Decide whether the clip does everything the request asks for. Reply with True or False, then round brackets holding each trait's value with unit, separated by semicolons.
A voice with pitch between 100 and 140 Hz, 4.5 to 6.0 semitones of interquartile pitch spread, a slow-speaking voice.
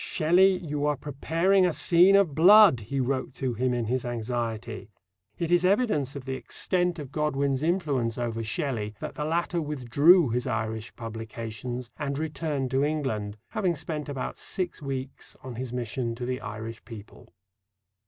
False (135 Hz; 5.2 semitones; 165 wpm)